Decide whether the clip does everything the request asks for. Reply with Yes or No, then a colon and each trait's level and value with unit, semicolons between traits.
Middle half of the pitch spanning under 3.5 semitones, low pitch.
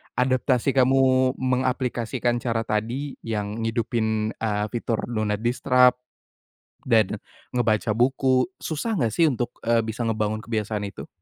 Yes: average, 2.7 semitones; low, 120 Hz